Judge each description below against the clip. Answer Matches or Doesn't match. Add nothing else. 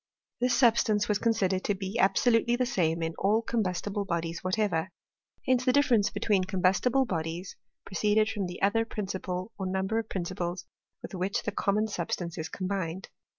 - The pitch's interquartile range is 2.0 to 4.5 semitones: Matches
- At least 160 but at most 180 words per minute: Matches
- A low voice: Doesn't match